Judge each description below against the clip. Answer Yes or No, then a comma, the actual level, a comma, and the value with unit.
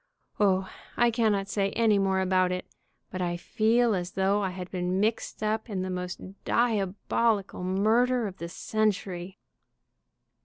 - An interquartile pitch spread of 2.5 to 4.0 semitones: Yes, average, 2.8 semitones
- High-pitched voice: Yes, high, 195 Hz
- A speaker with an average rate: Yes, average, 155 wpm